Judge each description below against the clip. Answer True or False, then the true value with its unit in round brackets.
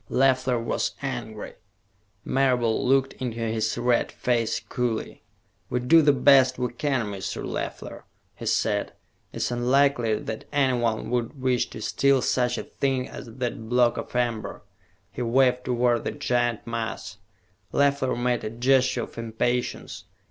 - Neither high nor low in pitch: False (125 Hz)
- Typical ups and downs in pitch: False (2.0 semitones)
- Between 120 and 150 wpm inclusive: True (145 wpm)